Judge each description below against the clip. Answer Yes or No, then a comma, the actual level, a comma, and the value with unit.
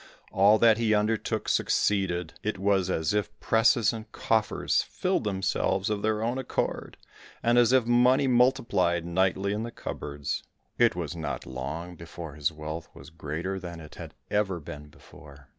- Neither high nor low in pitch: No, very low, 95 Hz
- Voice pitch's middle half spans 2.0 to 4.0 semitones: No, average, 5.3 semitones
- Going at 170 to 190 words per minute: No, average, 160 wpm